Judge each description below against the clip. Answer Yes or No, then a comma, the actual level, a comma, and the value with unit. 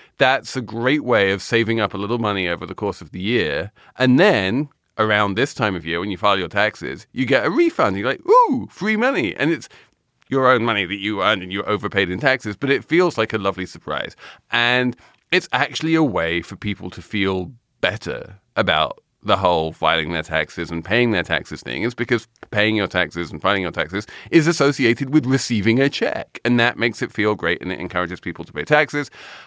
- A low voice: Yes, low, 110 Hz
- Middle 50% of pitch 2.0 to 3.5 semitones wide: No, wide, 5.5 semitones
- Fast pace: Yes, fast, 225 wpm